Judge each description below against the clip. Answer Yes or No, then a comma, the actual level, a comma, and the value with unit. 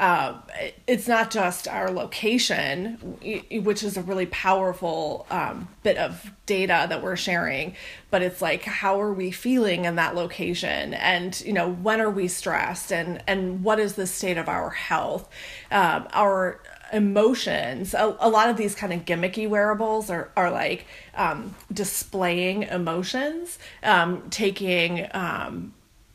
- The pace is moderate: Yes, average, 150 wpm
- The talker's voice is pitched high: Yes, high, 195 Hz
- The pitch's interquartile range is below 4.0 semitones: Yes, average, 3.0 semitones